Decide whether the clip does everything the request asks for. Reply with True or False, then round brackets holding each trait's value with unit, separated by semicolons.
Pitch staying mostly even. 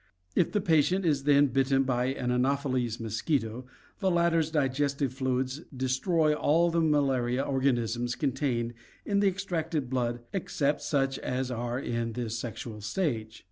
False (3.8 semitones)